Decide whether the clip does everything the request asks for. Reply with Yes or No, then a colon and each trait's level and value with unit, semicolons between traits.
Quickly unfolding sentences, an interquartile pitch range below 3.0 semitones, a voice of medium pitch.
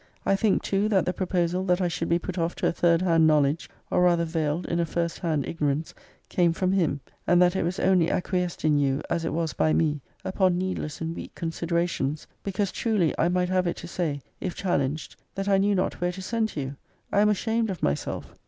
Yes: fast, 235 wpm; narrow, 2.6 semitones; medium, 175 Hz